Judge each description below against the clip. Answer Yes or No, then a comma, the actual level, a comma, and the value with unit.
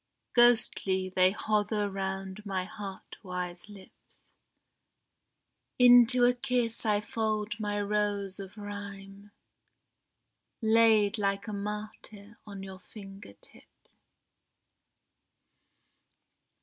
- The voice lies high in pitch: Yes, high, 205 Hz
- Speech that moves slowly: Yes, slow, 90 wpm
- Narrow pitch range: Yes, narrow, 1.8 semitones